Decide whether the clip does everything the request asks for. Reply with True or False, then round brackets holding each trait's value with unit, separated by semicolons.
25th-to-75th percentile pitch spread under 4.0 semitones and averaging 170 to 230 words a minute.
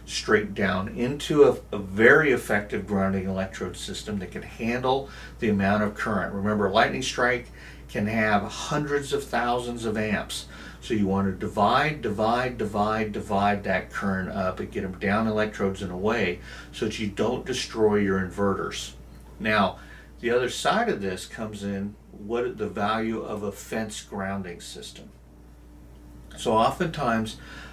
False (2.8 semitones; 155 wpm)